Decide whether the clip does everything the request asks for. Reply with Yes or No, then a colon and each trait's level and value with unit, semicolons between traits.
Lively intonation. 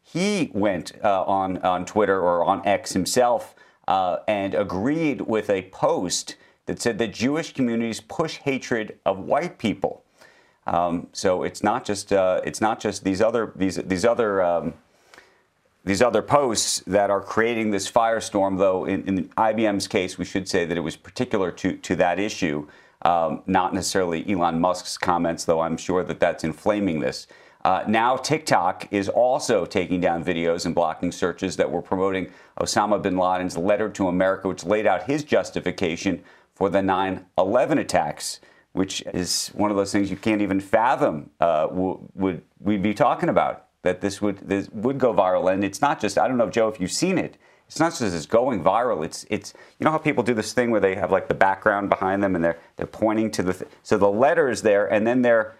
No: average, 2.8 semitones